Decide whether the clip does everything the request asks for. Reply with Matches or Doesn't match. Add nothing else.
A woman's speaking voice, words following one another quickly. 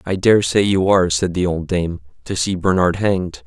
Doesn't match